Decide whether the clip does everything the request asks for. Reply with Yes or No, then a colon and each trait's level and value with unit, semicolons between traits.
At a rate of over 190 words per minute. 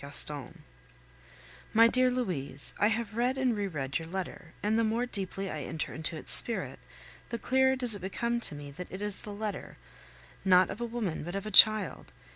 Yes: average, 200 wpm